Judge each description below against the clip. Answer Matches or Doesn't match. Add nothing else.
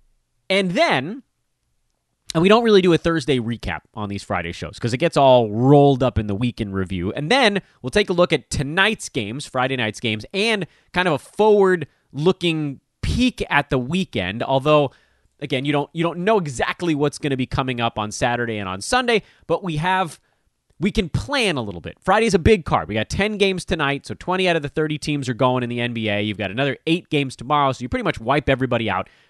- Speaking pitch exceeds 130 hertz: Matches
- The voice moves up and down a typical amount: Doesn't match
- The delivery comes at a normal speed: Doesn't match